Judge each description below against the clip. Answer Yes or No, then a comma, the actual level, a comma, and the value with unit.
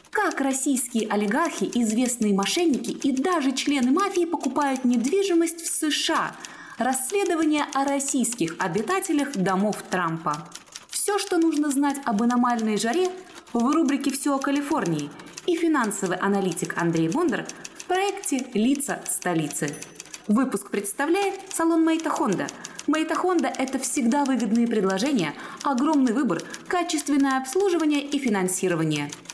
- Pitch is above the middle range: Yes, very high, 275 Hz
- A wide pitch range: Yes, wide, 6.7 semitones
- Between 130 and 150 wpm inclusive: No, slow, 110 wpm